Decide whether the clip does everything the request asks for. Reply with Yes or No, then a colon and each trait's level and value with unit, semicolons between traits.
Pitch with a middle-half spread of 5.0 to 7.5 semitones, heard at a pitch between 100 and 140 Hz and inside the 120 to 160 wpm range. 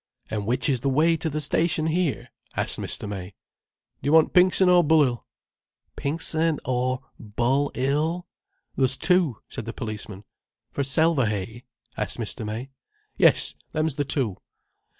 Yes: wide, 5.4 semitones; low, 135 Hz; average, 140 wpm